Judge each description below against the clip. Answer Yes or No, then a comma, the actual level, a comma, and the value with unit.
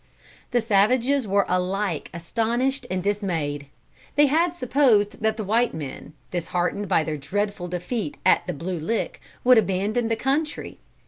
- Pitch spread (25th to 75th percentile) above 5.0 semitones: Yes, wide, 5.4 semitones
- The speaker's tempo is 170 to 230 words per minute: No, average, 145 wpm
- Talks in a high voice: Yes, high, 205 Hz